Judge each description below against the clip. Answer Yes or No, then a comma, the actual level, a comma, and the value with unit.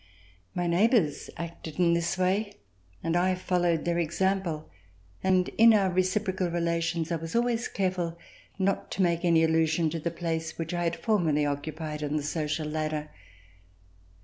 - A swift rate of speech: No, average, 160 wpm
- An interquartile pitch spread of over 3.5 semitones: No, narrow, 2.6 semitones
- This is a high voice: No, medium, 170 Hz